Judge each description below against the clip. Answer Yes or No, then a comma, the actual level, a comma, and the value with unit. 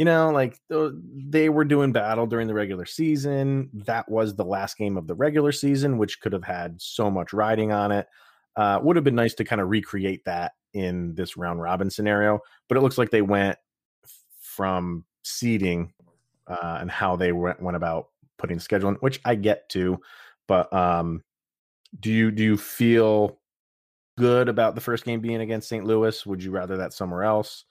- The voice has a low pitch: Yes, low, 105 Hz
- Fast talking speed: No, average, 195 wpm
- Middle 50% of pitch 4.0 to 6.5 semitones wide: Yes, average, 4.5 semitones